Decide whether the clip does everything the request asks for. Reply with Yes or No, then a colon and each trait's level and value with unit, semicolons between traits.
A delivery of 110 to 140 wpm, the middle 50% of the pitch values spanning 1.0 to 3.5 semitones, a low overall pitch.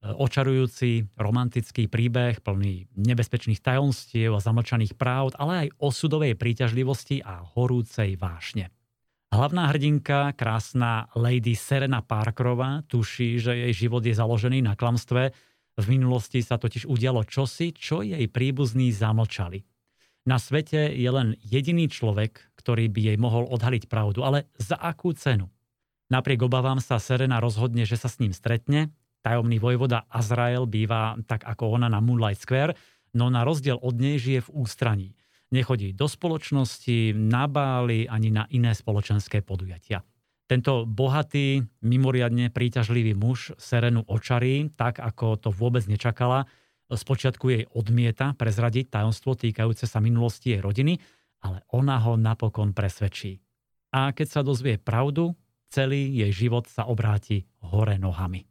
Yes: average, 135 wpm; average, 2.8 semitones; low, 120 Hz